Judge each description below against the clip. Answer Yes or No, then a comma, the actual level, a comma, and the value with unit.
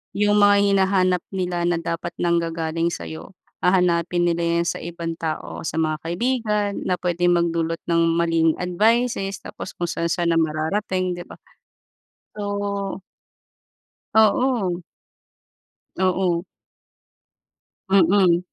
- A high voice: No, medium, 175 Hz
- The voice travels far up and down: No, average, 2.8 semitones